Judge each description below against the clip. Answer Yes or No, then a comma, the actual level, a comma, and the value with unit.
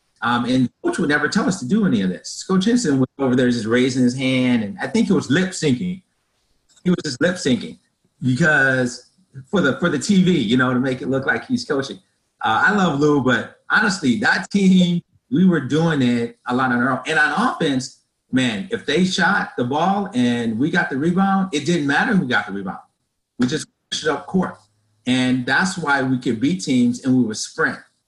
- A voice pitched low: No, medium, 150 Hz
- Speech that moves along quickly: Yes, fast, 220 wpm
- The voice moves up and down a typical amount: No, wide, 6.9 semitones